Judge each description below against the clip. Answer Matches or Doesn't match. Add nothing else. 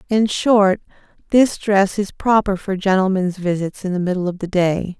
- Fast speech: Doesn't match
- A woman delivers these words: Matches